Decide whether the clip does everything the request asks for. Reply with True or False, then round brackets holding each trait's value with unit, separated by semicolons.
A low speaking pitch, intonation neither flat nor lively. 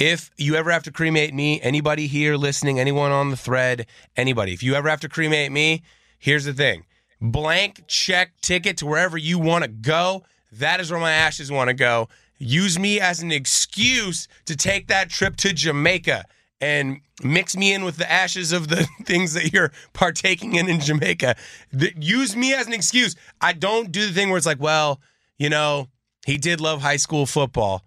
False (160 Hz; 4.1 semitones)